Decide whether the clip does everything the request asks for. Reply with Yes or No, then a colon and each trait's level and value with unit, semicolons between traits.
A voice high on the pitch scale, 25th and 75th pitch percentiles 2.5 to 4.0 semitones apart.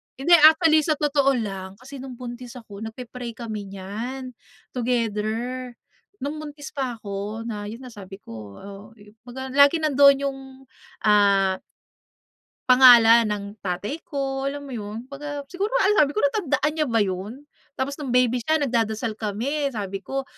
No: high, 245 Hz; average, 4.8 semitones